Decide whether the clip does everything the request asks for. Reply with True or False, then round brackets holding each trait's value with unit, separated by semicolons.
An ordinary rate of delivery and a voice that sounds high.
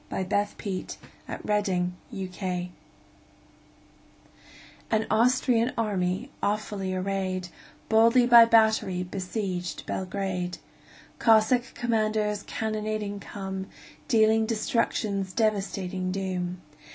False (85 wpm; 205 Hz)